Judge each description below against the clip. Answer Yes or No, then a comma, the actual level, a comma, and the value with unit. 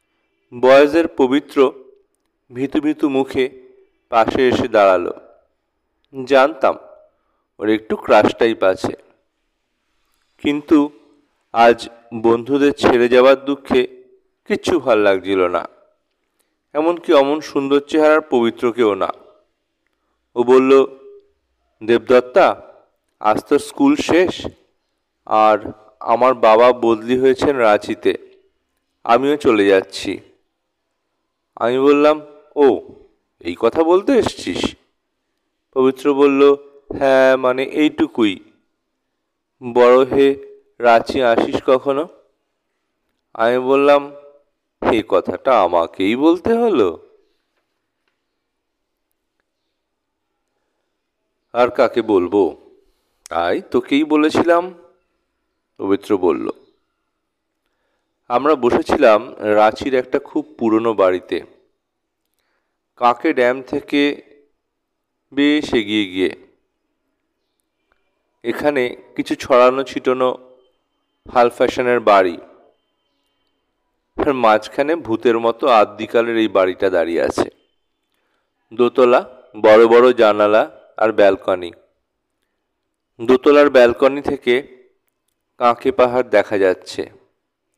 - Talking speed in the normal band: Yes, average, 80 wpm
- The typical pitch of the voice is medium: Yes, medium, 145 Hz